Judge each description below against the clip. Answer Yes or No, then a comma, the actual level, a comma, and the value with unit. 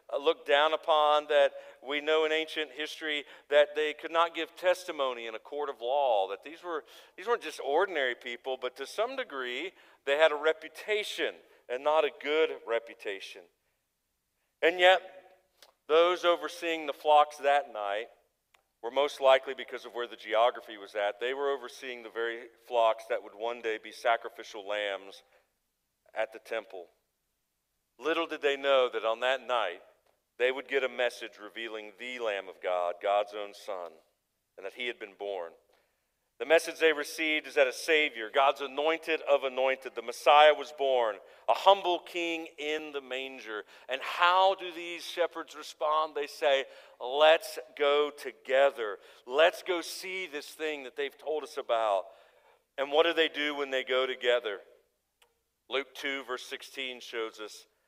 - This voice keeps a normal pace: Yes, average, 165 wpm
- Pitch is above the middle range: No, medium, 145 Hz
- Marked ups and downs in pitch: No, average, 4.3 semitones